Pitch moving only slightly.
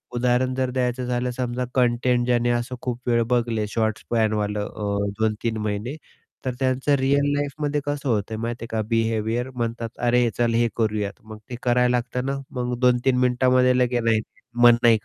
Yes: narrow, 1.9 semitones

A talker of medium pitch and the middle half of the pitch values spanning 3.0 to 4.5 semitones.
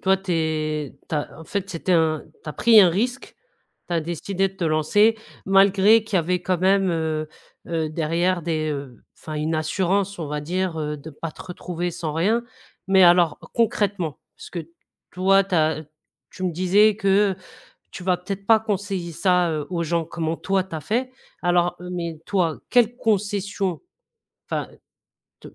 Yes: medium, 180 Hz; average, 3.4 semitones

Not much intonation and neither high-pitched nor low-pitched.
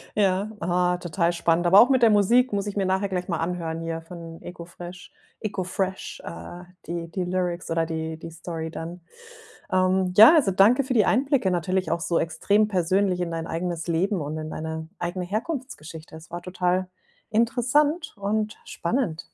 No: average, 3.5 semitones; medium, 180 Hz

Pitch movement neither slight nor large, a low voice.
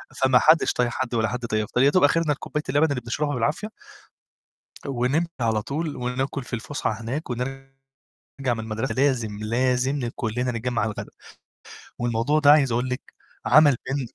Yes: average, 3.4 semitones; low, 125 Hz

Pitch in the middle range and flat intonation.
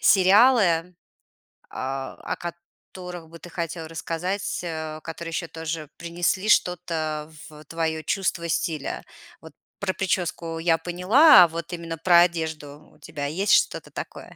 Yes: medium, 170 Hz; narrow, 2.0 semitones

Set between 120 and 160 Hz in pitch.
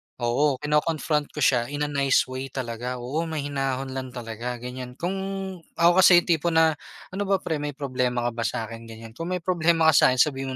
Yes: low, 135 Hz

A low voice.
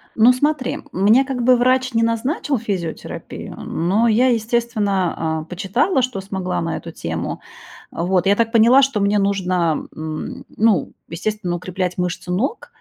No: high, 205 Hz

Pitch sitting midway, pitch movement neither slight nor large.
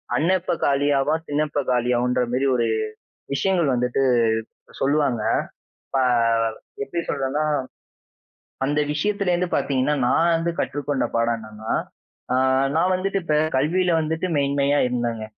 Yes: medium, 145 Hz; average, 4.5 semitones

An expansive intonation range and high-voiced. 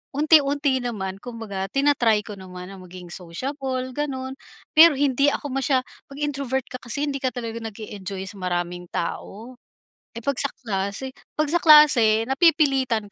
Yes: wide, 5.7 semitones; very high, 255 Hz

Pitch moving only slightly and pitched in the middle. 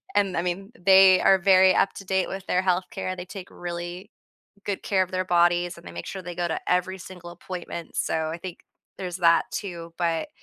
Yes: narrow, 1.6 semitones; medium, 180 Hz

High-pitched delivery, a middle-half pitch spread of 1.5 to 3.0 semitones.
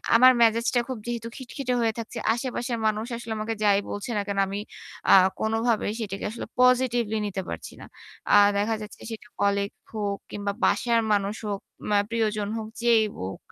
Yes: high, 220 Hz; narrow, 2.5 semitones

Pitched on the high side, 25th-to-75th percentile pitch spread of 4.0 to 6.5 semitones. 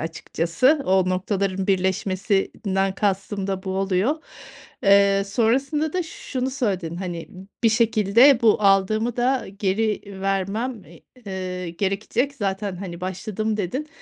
No: high, 195 Hz; average, 3.3 semitones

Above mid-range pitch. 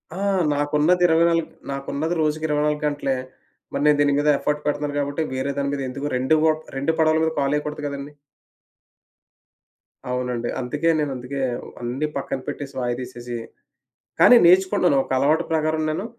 No: medium, 145 Hz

